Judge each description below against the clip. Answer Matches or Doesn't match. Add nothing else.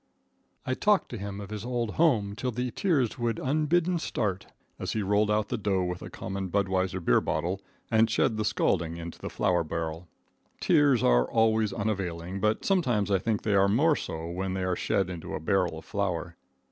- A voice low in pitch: Matches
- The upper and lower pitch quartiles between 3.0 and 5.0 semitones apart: Matches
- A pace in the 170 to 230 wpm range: Matches